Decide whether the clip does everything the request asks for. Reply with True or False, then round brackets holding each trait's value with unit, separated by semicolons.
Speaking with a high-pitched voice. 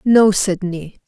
True (195 Hz)